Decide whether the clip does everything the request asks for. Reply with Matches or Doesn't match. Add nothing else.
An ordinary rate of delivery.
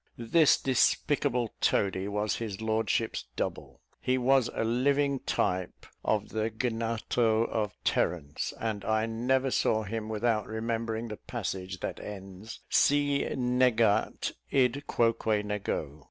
Doesn't match